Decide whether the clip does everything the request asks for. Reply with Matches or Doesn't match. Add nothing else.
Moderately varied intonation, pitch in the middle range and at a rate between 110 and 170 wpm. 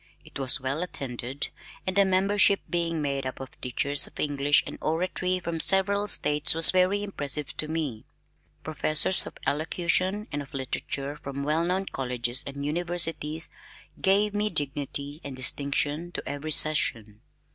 Matches